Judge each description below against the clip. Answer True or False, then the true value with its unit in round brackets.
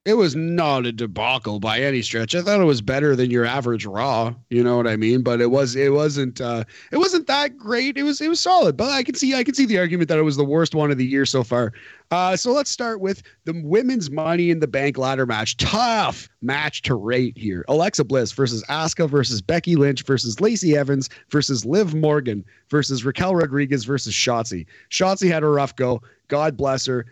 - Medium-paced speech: False (225 wpm)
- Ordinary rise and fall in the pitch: False (6.0 semitones)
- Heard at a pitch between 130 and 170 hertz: True (140 Hz)